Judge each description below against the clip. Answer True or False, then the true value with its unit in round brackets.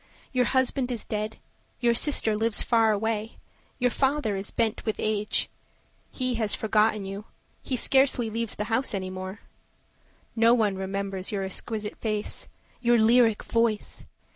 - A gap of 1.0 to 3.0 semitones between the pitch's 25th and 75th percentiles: True (2.4 semitones)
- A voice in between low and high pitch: False (220 Hz)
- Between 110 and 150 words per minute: True (145 wpm)